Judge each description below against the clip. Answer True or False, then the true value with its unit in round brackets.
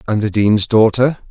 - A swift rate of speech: False (185 wpm)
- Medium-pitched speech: False (110 Hz)